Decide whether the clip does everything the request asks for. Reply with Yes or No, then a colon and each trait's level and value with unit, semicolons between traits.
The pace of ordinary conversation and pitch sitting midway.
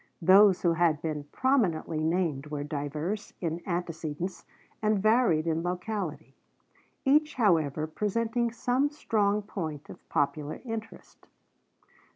No: slow, 115 wpm; medium, 175 Hz